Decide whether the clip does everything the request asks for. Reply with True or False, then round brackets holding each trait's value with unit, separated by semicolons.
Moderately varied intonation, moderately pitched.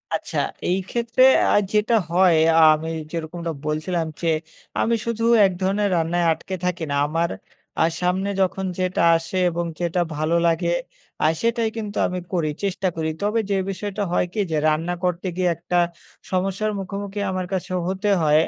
True (3.1 semitones; 180 Hz)